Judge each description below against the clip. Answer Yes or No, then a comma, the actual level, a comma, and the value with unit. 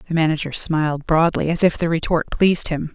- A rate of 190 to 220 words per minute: Yes, fast, 205 wpm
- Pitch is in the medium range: Yes, medium, 160 Hz